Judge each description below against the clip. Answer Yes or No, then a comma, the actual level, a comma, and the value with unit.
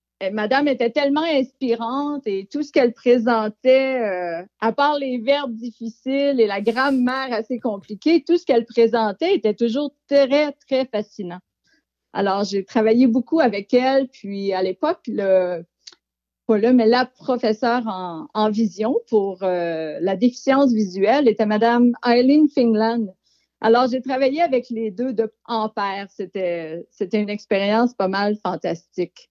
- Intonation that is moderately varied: Yes, average, 4.5 semitones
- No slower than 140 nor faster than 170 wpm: Yes, slow, 145 wpm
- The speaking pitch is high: Yes, high, 230 Hz